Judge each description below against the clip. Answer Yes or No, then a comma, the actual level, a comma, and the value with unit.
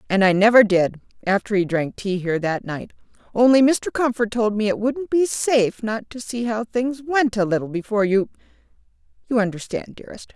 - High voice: Yes, high, 215 Hz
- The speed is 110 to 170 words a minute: No, average, 185 wpm